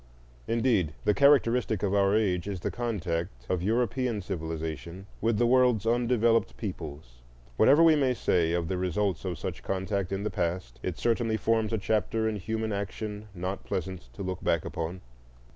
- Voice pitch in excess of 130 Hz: No, low, 100 Hz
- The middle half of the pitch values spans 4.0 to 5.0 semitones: Yes, average, 4.4 semitones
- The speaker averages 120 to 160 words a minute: No, average, 170 wpm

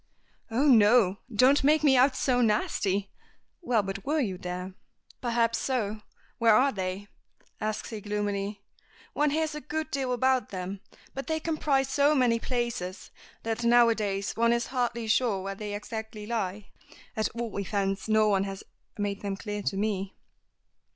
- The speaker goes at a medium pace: Yes, average, 165 wpm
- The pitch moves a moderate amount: Yes, average, 4.0 semitones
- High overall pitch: Yes, high, 220 Hz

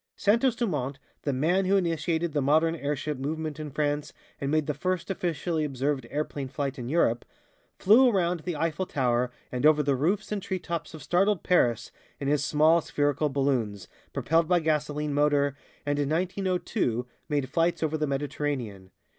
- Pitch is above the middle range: No, medium, 150 Hz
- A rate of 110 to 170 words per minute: Yes, average, 165 wpm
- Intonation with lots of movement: No, average, 3.4 semitones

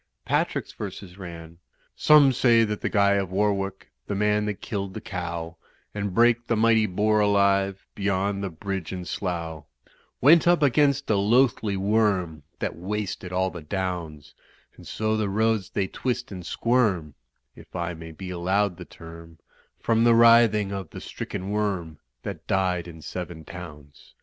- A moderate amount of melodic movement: Yes, average, 3.4 semitones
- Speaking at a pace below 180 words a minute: Yes, average, 160 wpm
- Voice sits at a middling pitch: No, low, 100 Hz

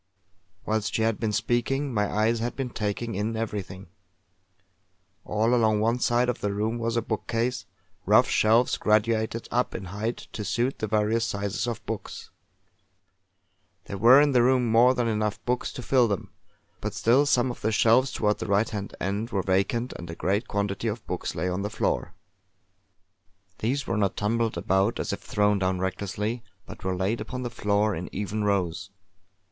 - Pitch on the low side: Yes, low, 110 Hz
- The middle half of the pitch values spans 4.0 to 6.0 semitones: No, narrow, 2.6 semitones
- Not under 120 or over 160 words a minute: No, average, 180 wpm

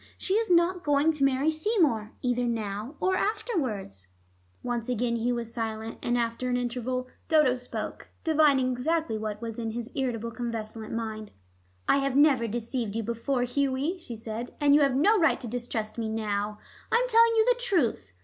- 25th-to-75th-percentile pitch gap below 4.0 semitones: No, average, 4.9 semitones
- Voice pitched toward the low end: No, high, 245 Hz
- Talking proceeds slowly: No, average, 180 wpm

